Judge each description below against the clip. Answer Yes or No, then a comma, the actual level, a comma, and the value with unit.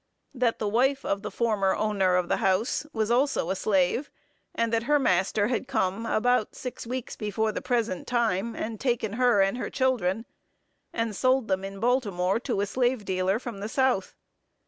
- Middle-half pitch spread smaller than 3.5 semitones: No, average, 4.1 semitones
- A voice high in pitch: Yes, high, 220 Hz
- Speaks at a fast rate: No, average, 185 wpm